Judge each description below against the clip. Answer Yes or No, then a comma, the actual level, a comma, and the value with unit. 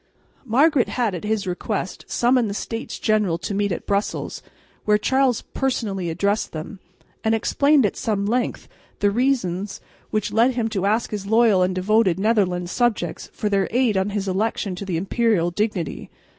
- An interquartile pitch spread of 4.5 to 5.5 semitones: No, average, 3.2 semitones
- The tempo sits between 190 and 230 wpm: No, average, 170 wpm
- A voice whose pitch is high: Yes, high, 210 Hz